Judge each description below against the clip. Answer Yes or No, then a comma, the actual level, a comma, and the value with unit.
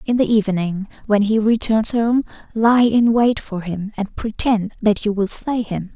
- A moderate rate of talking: Yes, average, 190 wpm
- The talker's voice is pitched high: Yes, high, 215 Hz